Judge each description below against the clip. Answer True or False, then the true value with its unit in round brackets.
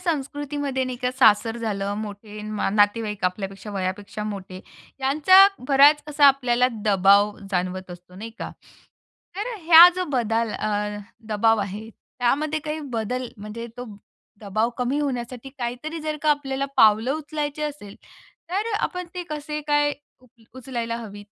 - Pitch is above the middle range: True (240 Hz)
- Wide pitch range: True (5.9 semitones)